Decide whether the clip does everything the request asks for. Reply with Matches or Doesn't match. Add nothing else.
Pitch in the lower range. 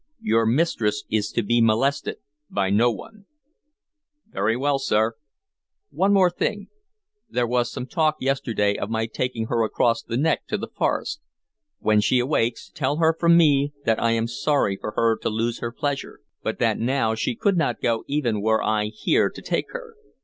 Matches